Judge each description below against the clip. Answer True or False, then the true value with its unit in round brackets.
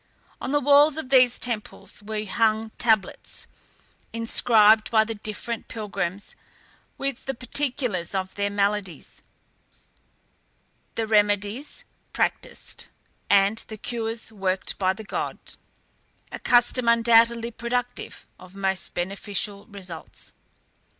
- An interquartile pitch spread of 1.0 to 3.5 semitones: True (2.8 semitones)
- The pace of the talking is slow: True (110 wpm)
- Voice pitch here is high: True (220 Hz)